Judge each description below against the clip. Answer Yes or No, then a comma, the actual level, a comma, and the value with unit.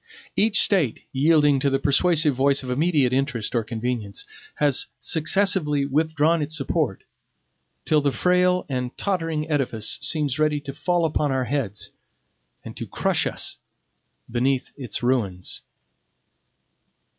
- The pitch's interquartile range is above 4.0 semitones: No, average, 3.7 semitones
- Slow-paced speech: Yes, slow, 130 wpm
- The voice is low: No, medium, 145 Hz